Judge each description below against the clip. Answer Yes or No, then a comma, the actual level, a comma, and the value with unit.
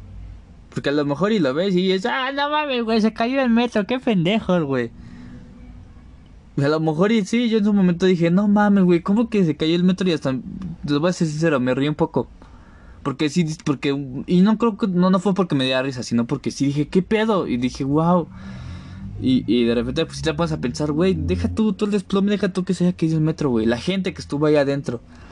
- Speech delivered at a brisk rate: Yes, fast, 245 wpm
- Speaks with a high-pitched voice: No, medium, 160 Hz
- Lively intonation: Yes, wide, 7.5 semitones